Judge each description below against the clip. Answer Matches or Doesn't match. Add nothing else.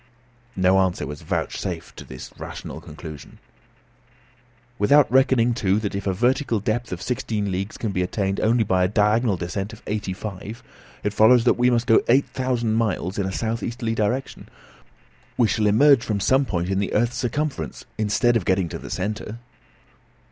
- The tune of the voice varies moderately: Matches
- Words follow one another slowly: Doesn't match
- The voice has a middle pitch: Doesn't match